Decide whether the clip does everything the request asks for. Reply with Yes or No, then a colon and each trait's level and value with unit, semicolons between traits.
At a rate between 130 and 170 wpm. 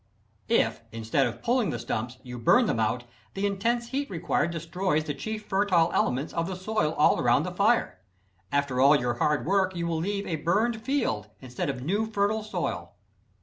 No: average, 190 wpm